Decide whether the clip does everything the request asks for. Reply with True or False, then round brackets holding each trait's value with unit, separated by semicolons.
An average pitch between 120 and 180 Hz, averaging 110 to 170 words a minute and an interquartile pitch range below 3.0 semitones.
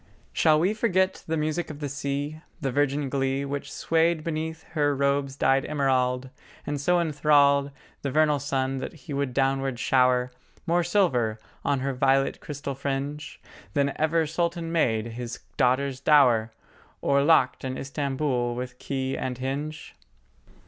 True (140 Hz; 150 wpm; 2.6 semitones)